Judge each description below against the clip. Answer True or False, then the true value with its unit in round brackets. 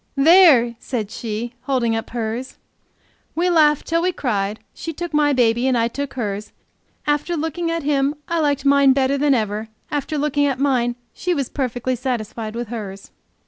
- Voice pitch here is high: True (265 Hz)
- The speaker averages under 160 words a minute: False (175 wpm)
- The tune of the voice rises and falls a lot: False (4.1 semitones)